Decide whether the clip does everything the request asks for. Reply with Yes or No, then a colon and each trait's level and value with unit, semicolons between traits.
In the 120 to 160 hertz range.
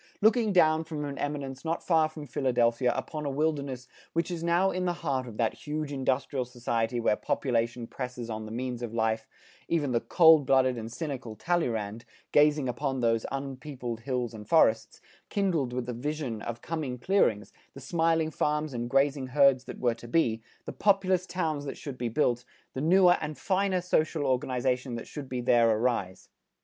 Yes: low, 135 Hz